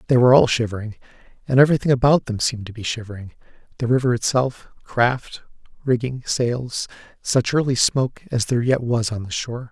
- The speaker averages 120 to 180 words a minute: Yes, average, 175 wpm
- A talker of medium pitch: No, low, 120 Hz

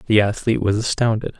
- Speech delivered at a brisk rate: No, average, 175 wpm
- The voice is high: No, low, 110 Hz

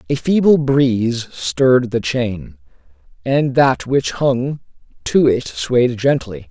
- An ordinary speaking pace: No, slow, 130 wpm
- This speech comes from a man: Yes, male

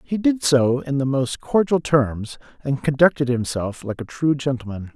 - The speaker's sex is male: Yes, male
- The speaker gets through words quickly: No, average, 180 wpm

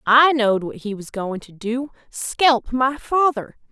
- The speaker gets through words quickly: No, average, 160 wpm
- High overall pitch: Yes, high, 245 Hz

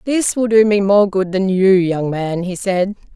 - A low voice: No, high, 195 Hz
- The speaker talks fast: Yes, fast, 230 wpm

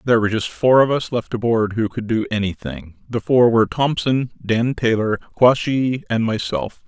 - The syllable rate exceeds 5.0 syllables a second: No, 4.9 syllables/s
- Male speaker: Yes, male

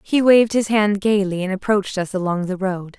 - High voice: Yes, high, 200 Hz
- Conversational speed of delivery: No, fast, 220 wpm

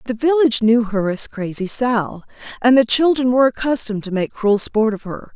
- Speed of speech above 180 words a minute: Yes, average, 200 wpm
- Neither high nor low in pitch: No, high, 230 Hz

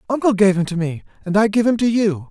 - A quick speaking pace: Yes, fast, 285 wpm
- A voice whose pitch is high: Yes, high, 200 Hz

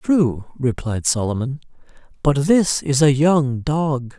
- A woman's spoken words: No, male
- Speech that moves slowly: Yes, slow, 130 wpm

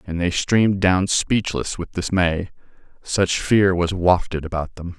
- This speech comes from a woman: No, male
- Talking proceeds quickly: No, average, 155 wpm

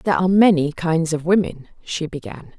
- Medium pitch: Yes, medium, 165 Hz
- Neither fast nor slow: Yes, average, 185 wpm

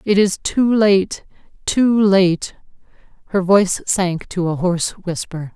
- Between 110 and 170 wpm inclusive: Yes, average, 140 wpm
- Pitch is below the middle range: No, high, 190 Hz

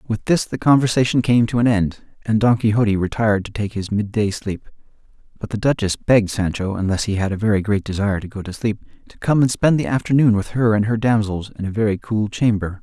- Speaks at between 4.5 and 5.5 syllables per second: No, 5.9 syllables/s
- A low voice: Yes, low, 110 Hz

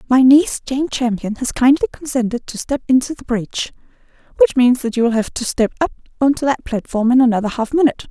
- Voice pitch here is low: No, very high, 250 Hz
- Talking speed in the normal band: No, fast, 215 wpm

